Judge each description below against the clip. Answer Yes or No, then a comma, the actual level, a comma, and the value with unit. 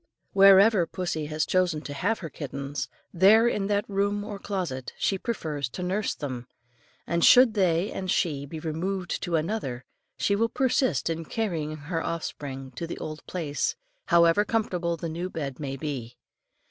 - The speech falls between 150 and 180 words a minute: Yes, average, 170 wpm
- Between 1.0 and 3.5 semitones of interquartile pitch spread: No, average, 4.7 semitones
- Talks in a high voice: No, medium, 170 Hz